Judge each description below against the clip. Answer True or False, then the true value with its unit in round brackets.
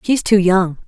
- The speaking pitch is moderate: False (195 Hz)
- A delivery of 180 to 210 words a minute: True (205 wpm)